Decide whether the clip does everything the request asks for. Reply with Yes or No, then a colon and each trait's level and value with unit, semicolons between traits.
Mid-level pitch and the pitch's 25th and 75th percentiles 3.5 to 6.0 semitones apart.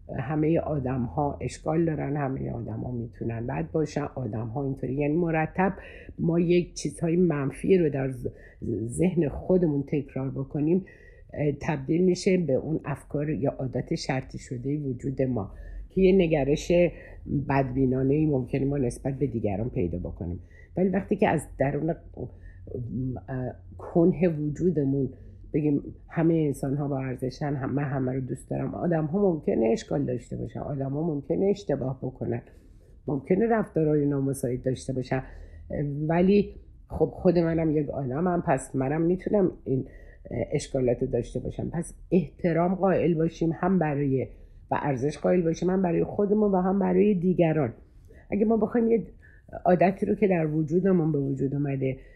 Yes: medium, 145 Hz; average, 4.7 semitones